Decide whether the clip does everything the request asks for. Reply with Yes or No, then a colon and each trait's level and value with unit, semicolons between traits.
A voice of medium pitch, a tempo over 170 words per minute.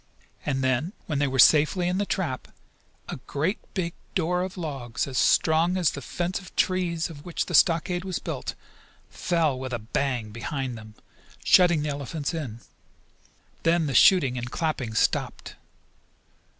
No: medium, 155 Hz; average, 160 wpm